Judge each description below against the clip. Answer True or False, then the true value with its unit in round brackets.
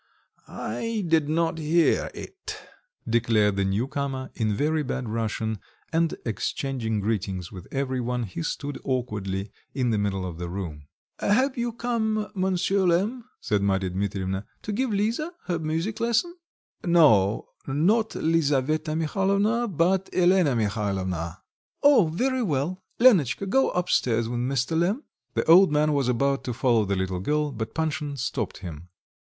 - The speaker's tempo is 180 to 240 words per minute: False (150 wpm)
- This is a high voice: False (140 Hz)